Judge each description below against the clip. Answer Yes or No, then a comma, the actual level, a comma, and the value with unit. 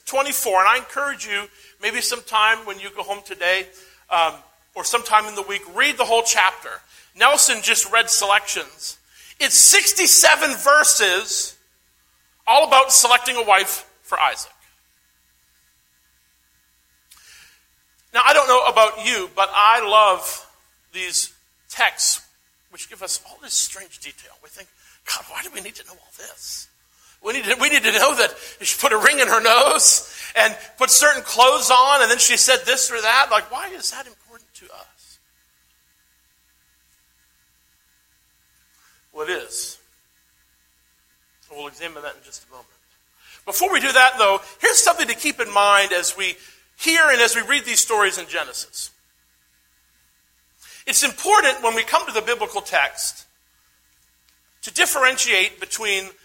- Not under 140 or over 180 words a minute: Yes, average, 155 wpm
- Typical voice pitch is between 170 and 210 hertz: Yes, high, 190 Hz